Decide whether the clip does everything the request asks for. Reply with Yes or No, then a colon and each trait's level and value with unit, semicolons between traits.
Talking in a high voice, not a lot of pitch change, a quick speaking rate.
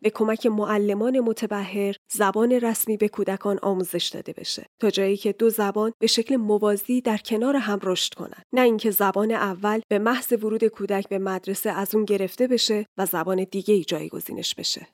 Yes: high, 210 Hz; narrow, 2.1 semitones; fast, 175 wpm